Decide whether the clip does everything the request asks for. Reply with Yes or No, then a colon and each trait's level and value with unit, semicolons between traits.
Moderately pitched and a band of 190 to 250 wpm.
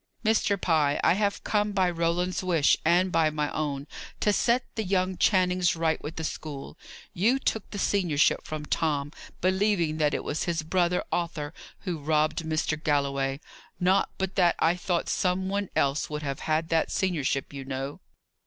No: medium, 165 Hz; average, 170 wpm